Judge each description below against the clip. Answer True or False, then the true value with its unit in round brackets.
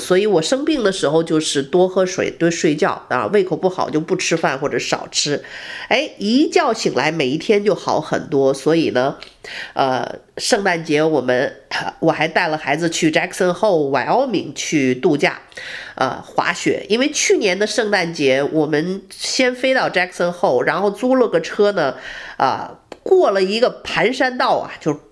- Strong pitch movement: True (6.9 semitones)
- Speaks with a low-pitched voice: False (185 Hz)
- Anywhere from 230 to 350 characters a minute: True (295 characters per minute)